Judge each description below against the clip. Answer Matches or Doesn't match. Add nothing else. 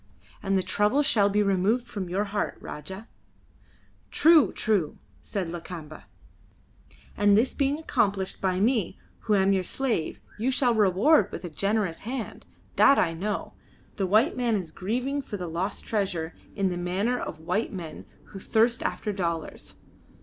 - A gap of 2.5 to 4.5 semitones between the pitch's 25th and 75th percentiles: Matches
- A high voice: Matches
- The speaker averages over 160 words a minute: Doesn't match